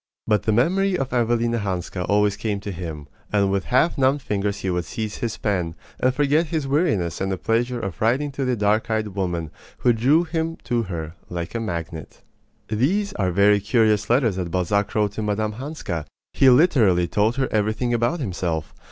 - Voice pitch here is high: No, low, 110 Hz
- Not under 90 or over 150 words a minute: No, average, 190 wpm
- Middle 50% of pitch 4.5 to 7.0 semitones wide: Yes, average, 4.9 semitones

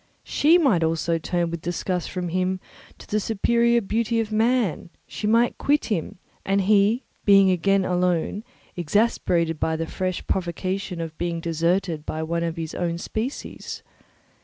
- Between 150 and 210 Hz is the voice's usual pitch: Yes, medium, 185 Hz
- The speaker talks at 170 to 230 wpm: No, average, 155 wpm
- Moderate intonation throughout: Yes, average, 4.2 semitones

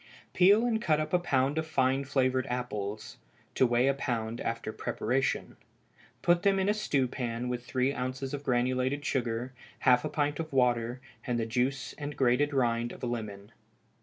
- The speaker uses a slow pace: No, average, 180 wpm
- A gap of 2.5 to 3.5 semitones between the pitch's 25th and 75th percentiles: Yes, average, 3.1 semitones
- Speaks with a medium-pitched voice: No, low, 130 Hz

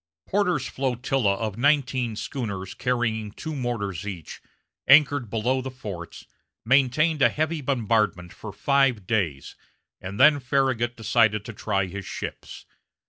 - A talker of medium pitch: No, low, 120 Hz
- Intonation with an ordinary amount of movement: Yes, average, 4.6 semitones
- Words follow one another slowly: Yes, slow, 130 wpm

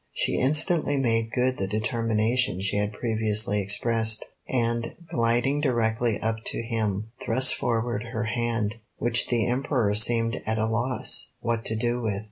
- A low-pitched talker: Yes, low, 115 Hz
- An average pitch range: No, narrow, 1.8 semitones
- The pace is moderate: Yes, average, 150 wpm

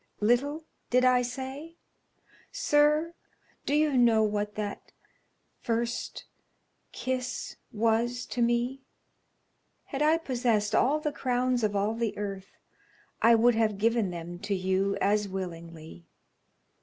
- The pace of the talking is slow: Yes, slow, 120 wpm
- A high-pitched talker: Yes, high, 235 Hz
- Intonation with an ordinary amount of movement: Yes, average, 3.9 semitones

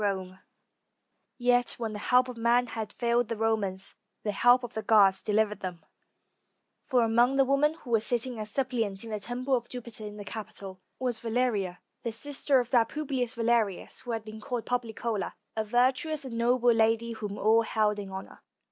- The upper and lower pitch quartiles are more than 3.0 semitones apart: No, average, 2.7 semitones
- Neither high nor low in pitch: No, high, 230 Hz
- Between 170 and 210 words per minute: Yes, average, 190 wpm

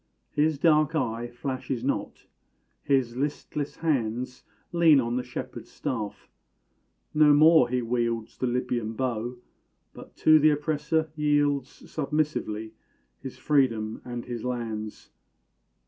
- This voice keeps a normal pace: No, slow, 115 wpm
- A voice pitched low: Yes, low, 130 Hz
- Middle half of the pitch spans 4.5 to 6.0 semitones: No, average, 3.9 semitones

